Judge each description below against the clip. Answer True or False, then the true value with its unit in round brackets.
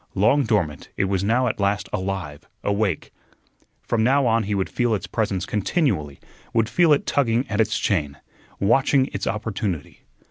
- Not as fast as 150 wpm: False (165 wpm)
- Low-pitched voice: True (105 Hz)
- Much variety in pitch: False (3.7 semitones)